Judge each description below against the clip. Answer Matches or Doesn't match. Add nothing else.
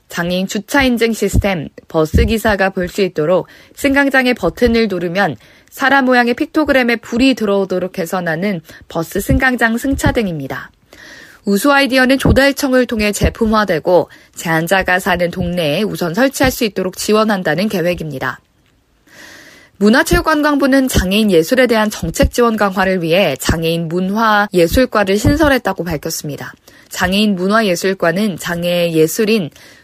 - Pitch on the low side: Doesn't match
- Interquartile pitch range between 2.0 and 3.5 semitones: Doesn't match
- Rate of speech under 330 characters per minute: Doesn't match